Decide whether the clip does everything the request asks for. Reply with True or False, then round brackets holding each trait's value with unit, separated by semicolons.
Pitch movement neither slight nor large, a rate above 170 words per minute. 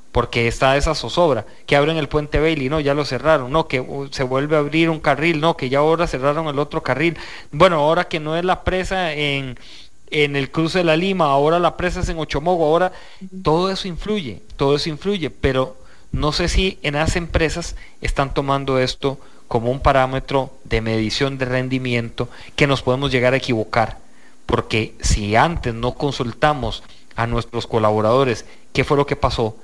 True (3.9 semitones; 185 wpm)